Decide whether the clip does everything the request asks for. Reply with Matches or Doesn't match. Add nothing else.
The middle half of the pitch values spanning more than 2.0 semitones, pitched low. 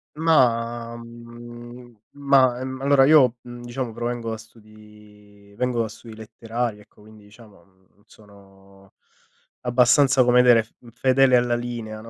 Matches